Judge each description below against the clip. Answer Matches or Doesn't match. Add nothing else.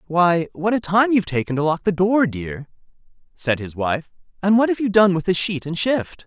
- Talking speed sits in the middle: Doesn't match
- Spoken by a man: Matches